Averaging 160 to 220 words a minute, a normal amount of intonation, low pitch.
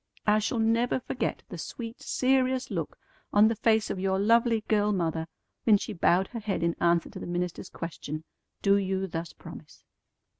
No: average, 180 wpm; average, 4.5 semitones; high, 205 Hz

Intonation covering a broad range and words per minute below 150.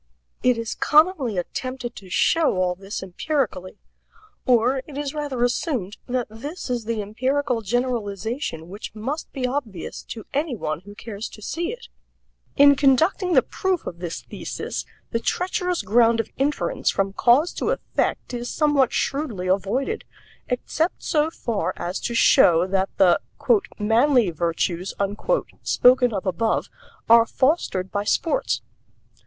Yes: wide, 6.2 semitones; average, 140 wpm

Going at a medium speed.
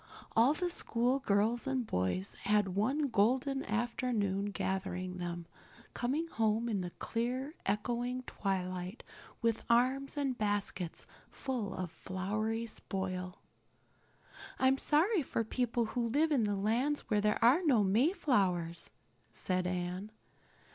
No: slow, 125 wpm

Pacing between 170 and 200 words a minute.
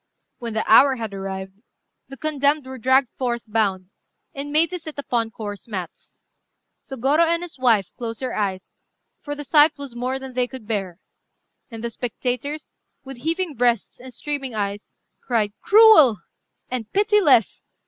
No: average, 160 wpm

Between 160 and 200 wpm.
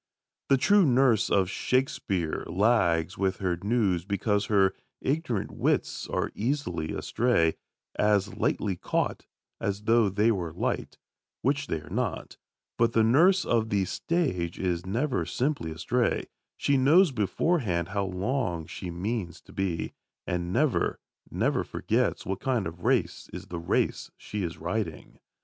No: average, 145 wpm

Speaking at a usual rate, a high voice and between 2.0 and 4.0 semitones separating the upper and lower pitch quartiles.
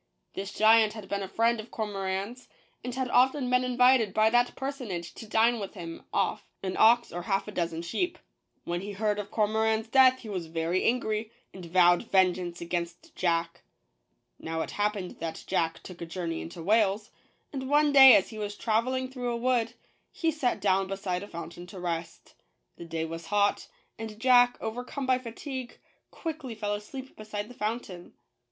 No: average, 185 wpm; high, 210 Hz; average, 5.1 semitones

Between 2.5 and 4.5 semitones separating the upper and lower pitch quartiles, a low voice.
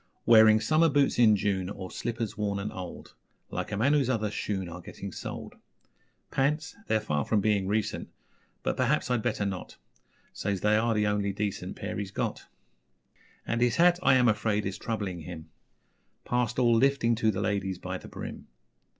Yes: average, 3.2 semitones; low, 105 Hz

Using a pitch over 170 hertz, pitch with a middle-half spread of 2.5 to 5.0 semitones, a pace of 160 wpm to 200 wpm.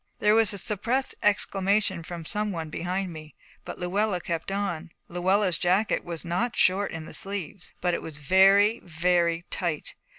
Yes: medium, 185 Hz; average, 3.1 semitones; average, 165 wpm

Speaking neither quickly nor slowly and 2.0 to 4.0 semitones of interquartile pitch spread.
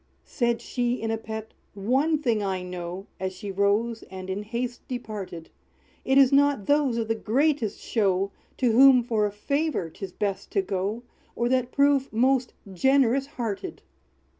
No: average, 165 wpm; average, 4.7 semitones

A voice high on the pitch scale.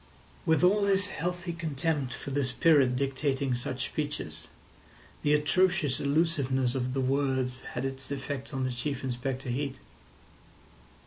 No: medium, 140 Hz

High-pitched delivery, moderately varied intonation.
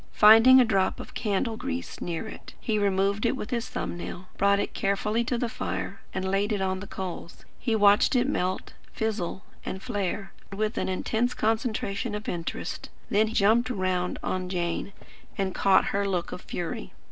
Yes: high, 200 Hz; average, 3.0 semitones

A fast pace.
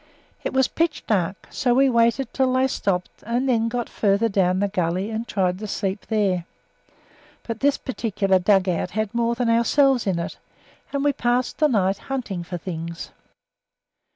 No: average, 175 wpm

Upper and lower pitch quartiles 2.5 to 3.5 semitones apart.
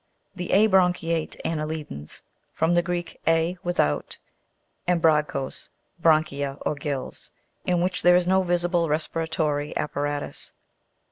Yes: average, 3.0 semitones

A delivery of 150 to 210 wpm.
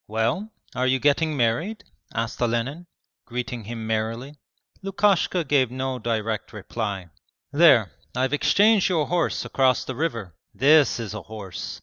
No: slow, 135 wpm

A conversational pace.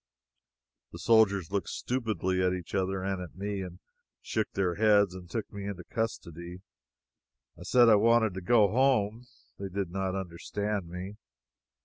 Yes: average, 155 wpm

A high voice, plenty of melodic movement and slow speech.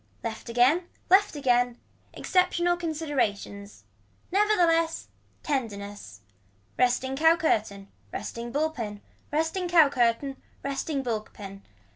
Yes: very high, 270 Hz; wide, 6.4 semitones; slow, 110 wpm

